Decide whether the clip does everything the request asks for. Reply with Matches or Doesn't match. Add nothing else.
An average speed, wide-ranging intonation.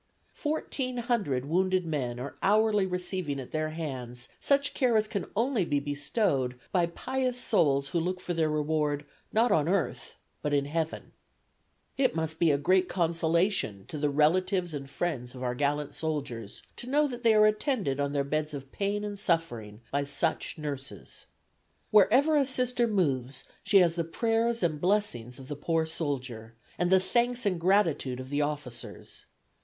Matches